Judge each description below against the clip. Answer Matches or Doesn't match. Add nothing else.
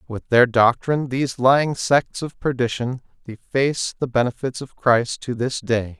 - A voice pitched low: Matches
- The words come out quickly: Doesn't match